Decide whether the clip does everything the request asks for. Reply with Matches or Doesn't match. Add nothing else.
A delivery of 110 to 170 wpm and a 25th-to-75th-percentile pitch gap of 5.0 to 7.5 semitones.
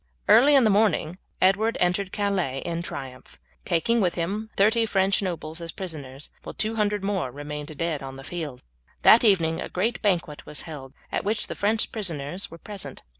Doesn't match